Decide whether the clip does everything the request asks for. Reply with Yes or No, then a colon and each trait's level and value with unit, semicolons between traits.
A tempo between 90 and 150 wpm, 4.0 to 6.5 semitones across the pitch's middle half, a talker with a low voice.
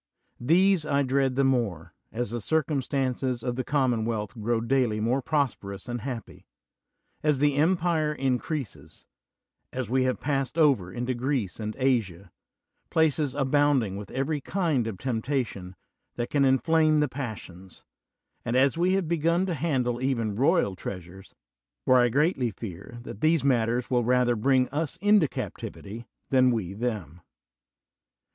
Yes: average, 145 wpm; average, 4.4 semitones; low, 130 Hz